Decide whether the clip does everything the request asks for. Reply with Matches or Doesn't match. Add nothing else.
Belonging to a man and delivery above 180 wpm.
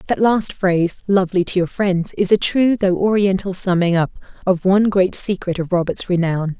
Doesn't match